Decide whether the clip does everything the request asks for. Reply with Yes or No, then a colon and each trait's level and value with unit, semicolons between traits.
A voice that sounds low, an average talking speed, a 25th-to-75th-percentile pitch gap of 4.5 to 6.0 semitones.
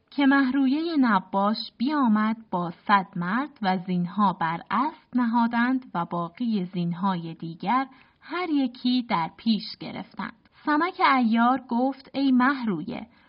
No: high, 235 Hz; average, 115 wpm; average, 5.3 semitones